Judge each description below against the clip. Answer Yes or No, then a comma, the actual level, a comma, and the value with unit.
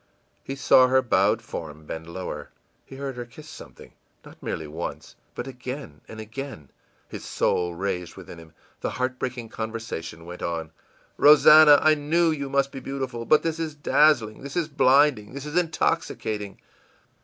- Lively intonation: Yes, wide, 6.8 semitones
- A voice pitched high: No, low, 130 Hz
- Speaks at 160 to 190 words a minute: Yes, average, 165 wpm